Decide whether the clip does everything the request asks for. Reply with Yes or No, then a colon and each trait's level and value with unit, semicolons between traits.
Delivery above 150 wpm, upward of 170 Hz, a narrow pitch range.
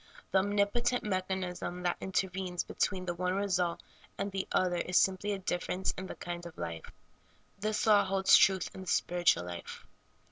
Yes: average, 170 wpm; medium, 185 Hz; narrow, 1.6 semitones